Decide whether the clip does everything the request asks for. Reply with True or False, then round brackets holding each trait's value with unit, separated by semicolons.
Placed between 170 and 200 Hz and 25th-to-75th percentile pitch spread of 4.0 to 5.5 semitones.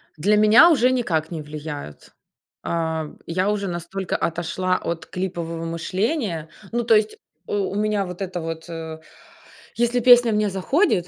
True (185 Hz; 4.4 semitones)